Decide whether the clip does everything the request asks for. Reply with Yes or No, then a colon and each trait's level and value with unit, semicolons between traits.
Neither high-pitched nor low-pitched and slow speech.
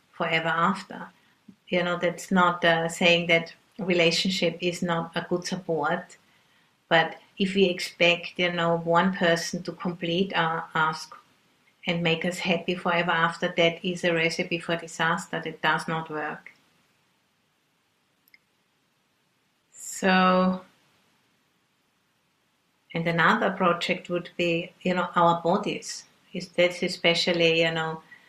Yes: medium, 175 Hz; slow, 120 wpm